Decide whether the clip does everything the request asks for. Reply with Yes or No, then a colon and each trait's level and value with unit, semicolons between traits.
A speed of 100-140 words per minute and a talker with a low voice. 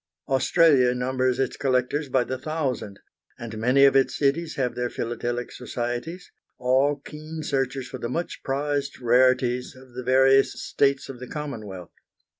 No: average, 150 wpm; low, 130 Hz